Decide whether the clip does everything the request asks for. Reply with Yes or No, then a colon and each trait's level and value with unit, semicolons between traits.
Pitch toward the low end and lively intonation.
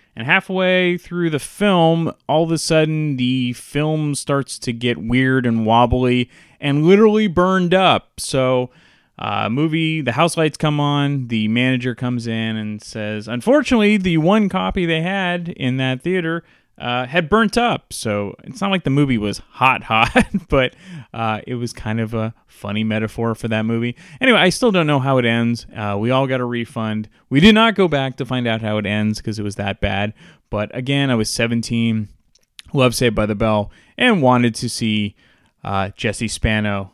Yes: low, 125 Hz; wide, 6.6 semitones